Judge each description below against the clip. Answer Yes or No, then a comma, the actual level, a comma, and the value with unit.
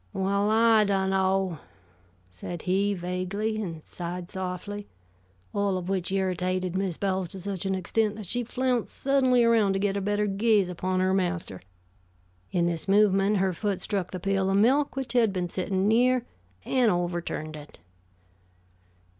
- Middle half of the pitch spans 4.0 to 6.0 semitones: No, narrow, 2.5 semitones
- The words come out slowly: No, average, 155 wpm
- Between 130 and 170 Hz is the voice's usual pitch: No, high, 195 Hz